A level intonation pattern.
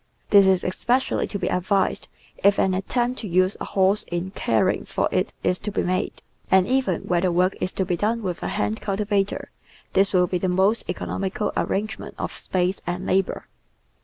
Yes: narrow, 2.0 semitones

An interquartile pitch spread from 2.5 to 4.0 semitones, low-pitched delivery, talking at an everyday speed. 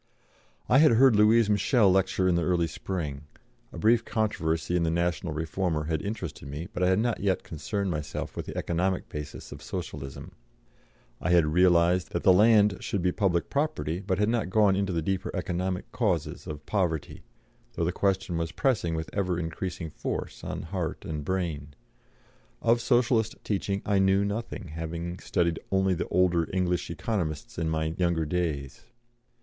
Yes: average, 3.5 semitones; very low, 90 Hz; average, 170 wpm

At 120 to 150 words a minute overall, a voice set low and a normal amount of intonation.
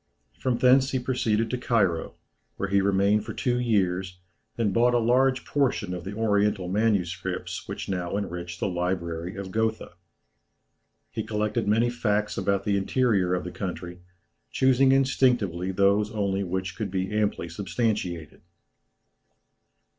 Yes: average, 140 wpm; low, 100 Hz; average, 4.0 semitones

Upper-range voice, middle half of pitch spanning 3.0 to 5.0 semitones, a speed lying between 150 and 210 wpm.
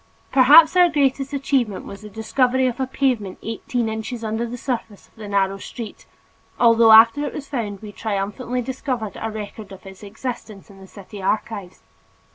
Yes: high, 225 Hz; average, 3.9 semitones; average, 175 wpm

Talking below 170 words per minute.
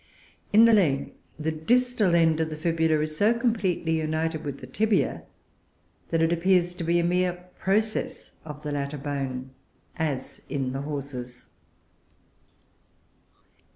Yes: average, 140 wpm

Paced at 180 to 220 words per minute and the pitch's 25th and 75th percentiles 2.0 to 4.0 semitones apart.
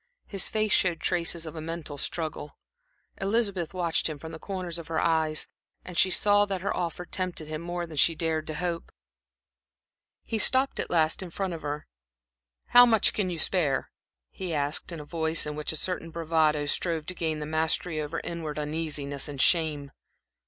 Yes: average, 190 wpm; narrow, 2.6 semitones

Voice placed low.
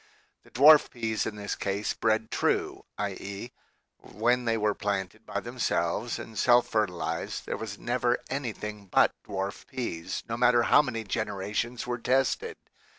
Yes: low, 110 Hz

